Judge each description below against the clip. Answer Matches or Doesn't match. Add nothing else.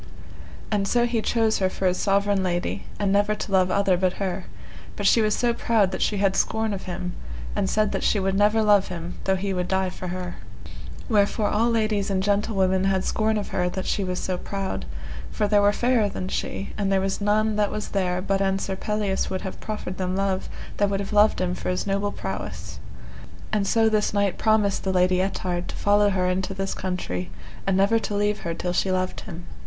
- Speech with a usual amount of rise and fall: Doesn't match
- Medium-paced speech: Doesn't match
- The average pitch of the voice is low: Doesn't match